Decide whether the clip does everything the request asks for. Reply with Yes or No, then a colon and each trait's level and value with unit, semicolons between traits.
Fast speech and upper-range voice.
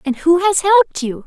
Yes: fast, 235 wpm; very high, 330 Hz